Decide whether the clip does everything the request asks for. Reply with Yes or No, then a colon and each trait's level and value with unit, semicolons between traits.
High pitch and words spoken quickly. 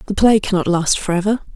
No: high, 195 Hz; average, 195 wpm